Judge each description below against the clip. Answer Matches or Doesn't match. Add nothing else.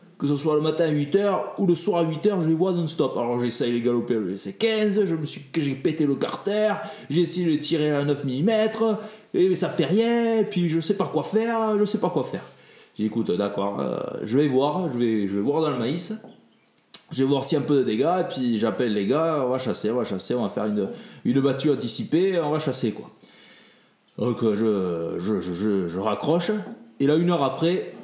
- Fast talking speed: Matches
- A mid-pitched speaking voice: Matches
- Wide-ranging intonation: Matches